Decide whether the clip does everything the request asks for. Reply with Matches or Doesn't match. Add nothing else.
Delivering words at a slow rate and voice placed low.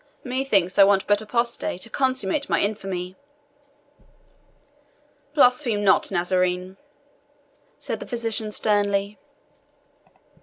Doesn't match